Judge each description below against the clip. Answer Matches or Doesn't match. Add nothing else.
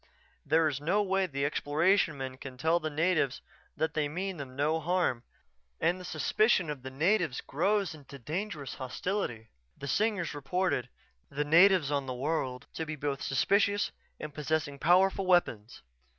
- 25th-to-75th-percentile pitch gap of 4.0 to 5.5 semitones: Matches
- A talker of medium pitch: Matches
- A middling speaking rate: Matches